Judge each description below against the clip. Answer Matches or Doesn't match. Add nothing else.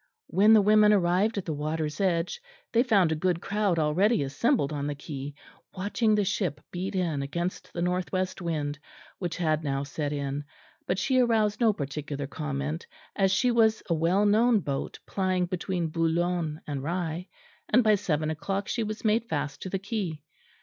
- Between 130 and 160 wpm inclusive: Doesn't match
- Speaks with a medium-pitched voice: Matches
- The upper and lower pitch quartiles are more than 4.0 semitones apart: Matches